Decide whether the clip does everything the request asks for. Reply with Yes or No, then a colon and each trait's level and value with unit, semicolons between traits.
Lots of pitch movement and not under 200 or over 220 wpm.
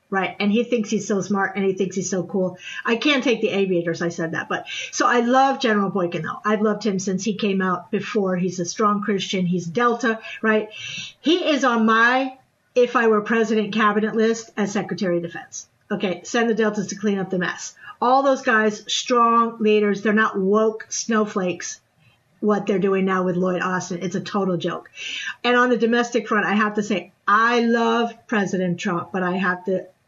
No: average, 3.5 semitones; fast, 205 wpm